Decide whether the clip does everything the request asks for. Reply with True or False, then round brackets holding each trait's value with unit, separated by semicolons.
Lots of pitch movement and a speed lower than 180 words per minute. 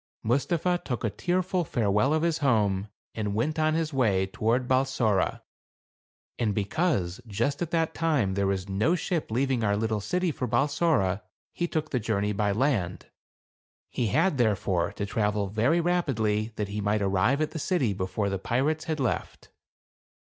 True (7.3 semitones; 170 wpm)